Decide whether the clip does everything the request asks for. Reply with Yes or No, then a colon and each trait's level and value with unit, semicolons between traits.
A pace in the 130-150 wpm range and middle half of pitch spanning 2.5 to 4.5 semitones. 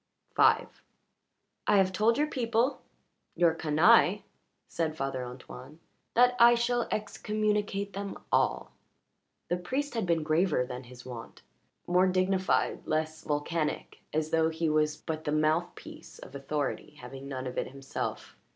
No: average, 140 wpm; wide, 5.5 semitones